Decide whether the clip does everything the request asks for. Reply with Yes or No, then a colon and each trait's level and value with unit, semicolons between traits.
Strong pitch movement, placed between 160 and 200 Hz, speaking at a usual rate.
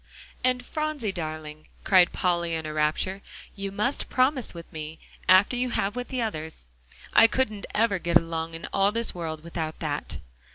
Yes: wide, 6.2 semitones; medium, 185 Hz; average, 170 wpm